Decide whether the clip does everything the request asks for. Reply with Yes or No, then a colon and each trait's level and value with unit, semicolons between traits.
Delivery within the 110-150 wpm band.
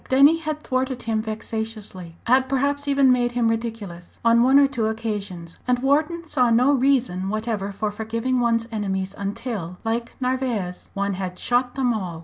No: average, 165 wpm